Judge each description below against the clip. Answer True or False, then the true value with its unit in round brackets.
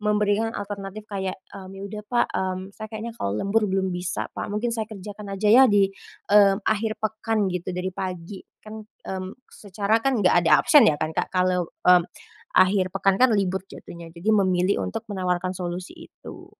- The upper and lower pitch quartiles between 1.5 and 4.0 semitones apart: True (2.7 semitones)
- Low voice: False (195 Hz)